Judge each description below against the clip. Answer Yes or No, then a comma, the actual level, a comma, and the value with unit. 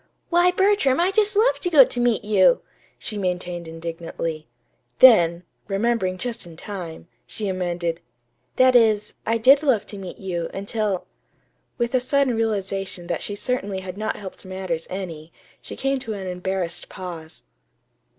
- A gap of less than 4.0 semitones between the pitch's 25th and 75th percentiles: No, wide, 5.5 semitones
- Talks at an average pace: Yes, average, 160 wpm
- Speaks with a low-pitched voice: No, high, 200 Hz